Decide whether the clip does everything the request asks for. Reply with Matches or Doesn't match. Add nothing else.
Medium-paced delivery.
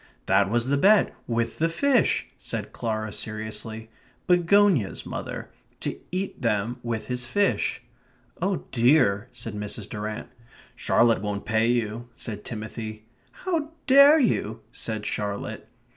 Doesn't match